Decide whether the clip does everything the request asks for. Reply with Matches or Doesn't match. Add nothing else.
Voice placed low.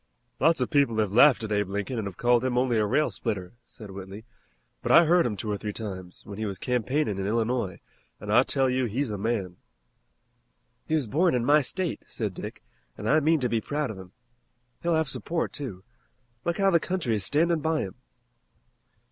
Matches